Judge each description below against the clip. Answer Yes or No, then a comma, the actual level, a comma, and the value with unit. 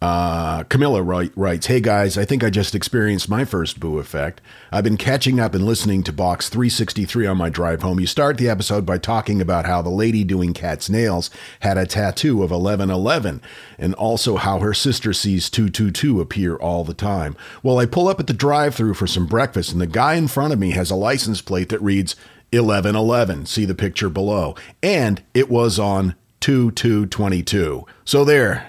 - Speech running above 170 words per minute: Yes, average, 195 wpm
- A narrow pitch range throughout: No, average, 4.2 semitones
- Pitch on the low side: Yes, low, 100 Hz